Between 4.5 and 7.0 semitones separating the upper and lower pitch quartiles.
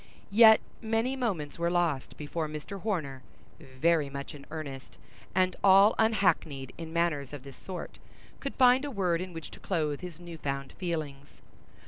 Yes: average, 5.2 semitones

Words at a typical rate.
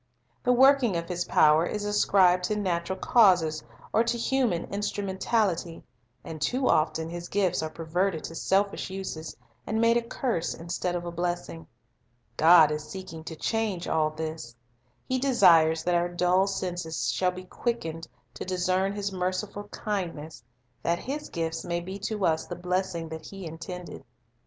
Yes: average, 160 wpm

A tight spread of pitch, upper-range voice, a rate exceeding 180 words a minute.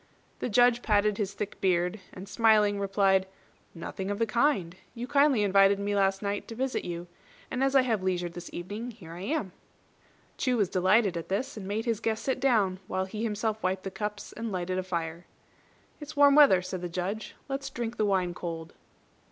No: average, 3.8 semitones; high, 205 Hz; average, 200 wpm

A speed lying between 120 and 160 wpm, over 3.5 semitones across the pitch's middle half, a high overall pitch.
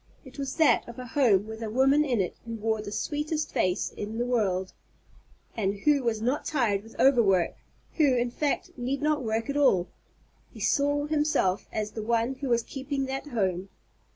No: average, 190 wpm; average, 4.7 semitones; high, 240 Hz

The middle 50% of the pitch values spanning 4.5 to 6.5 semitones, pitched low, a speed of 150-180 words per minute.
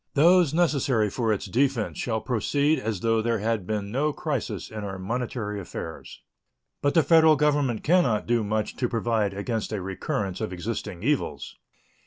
Yes: average, 5.2 semitones; low, 115 Hz; average, 170 wpm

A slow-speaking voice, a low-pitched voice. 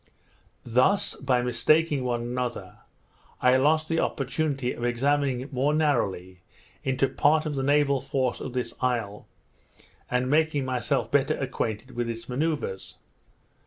Yes: slow, 130 wpm; low, 130 Hz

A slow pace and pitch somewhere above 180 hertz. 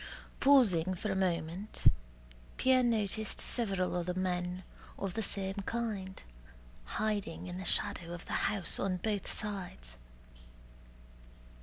Yes: slow, 120 wpm; high, 190 Hz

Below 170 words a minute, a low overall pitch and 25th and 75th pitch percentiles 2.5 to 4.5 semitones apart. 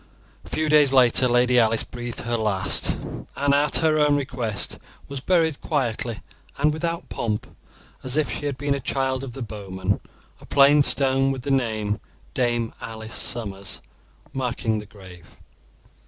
Yes: average, 155 wpm; low, 125 Hz; average, 4.2 semitones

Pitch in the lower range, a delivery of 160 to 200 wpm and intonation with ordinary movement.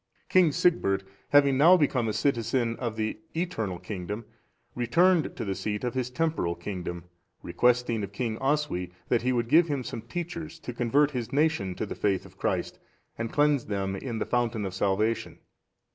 No: low, 120 Hz; average, 175 wpm; wide, 5.7 semitones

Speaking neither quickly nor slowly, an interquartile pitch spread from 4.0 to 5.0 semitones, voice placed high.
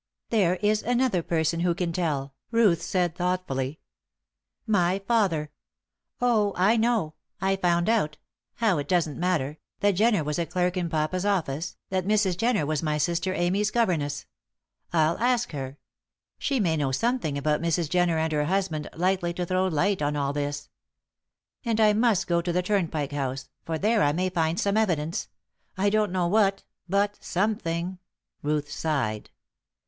No: average, 165 wpm; average, 4.7 semitones; medium, 175 Hz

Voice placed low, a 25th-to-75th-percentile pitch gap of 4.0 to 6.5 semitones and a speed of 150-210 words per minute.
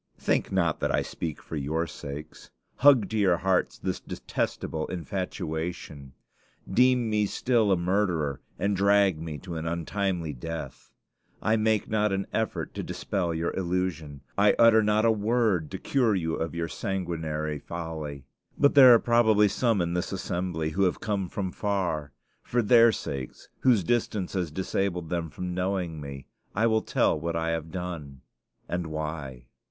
Yes: very low, 90 Hz; average, 4.6 semitones; average, 160 wpm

